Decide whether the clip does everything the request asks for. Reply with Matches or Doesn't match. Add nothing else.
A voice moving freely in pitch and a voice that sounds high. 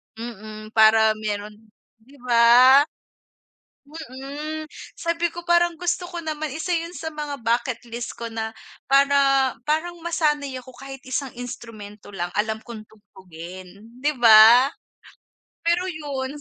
Matches